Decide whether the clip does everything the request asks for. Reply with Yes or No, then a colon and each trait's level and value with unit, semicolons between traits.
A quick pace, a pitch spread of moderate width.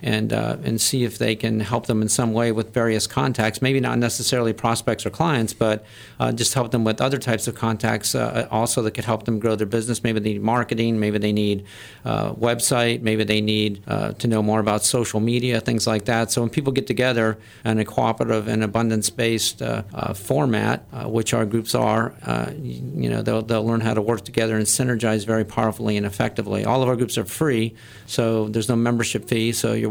No: fast, 220 wpm; narrow, 1.5 semitones